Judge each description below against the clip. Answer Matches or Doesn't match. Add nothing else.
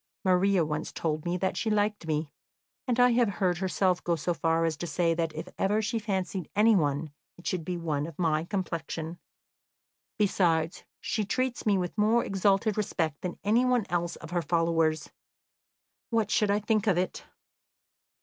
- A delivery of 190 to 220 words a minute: Doesn't match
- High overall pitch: Doesn't match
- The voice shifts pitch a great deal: Doesn't match